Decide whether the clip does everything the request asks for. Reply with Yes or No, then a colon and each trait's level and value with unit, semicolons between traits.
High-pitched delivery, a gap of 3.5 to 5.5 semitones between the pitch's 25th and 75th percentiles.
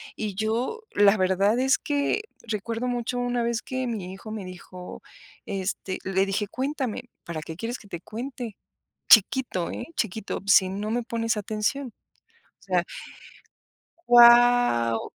Yes: high, 220 Hz; average, 4.1 semitones